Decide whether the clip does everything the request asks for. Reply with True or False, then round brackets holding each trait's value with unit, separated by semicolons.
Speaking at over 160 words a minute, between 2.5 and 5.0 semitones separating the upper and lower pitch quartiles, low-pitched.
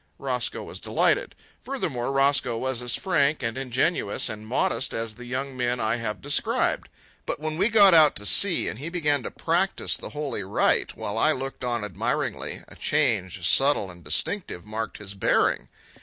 False (175 wpm; 5.4 semitones; 130 Hz)